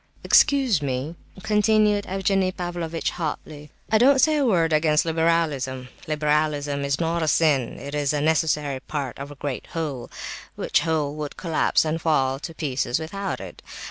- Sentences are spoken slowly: No, average, 160 wpm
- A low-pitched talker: No, medium, 155 Hz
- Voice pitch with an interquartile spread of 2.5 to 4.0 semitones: Yes, average, 3.2 semitones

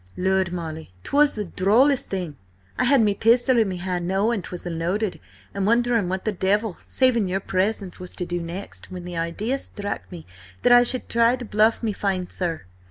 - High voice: Yes, high, 195 Hz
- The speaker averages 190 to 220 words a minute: Yes, average, 195 wpm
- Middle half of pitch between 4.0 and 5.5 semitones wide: Yes, average, 4.3 semitones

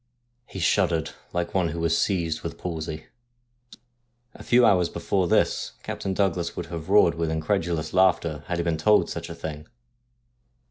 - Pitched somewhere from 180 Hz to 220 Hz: No, very low, 85 Hz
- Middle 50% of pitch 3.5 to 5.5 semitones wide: No, average, 2.7 semitones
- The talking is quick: No, average, 160 wpm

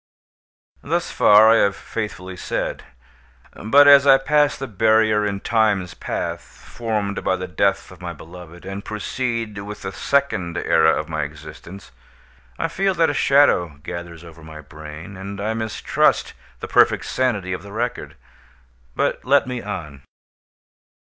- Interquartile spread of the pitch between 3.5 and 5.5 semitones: Yes, average, 4.7 semitones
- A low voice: Yes, low, 100 Hz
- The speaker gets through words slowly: No, average, 150 wpm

